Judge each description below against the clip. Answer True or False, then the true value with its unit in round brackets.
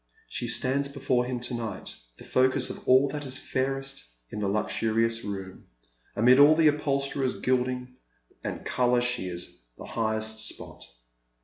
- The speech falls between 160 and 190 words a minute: False (150 wpm)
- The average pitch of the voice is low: True (125 Hz)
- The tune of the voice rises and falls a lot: False (3.4 semitones)